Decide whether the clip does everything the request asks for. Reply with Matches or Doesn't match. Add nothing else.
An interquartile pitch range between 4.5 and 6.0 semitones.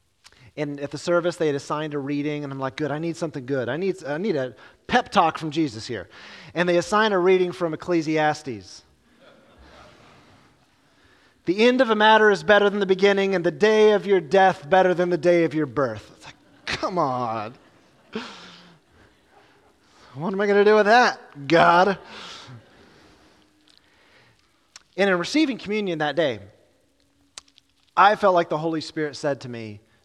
Matches